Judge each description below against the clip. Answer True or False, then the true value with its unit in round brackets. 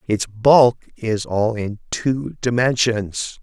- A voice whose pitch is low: True (115 Hz)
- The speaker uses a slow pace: True (125 wpm)